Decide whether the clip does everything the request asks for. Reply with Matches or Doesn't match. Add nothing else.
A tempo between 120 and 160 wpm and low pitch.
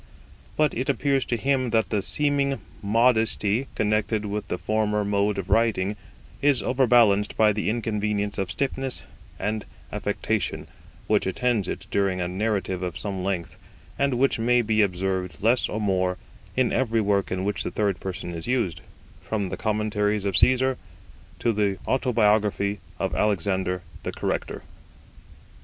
Matches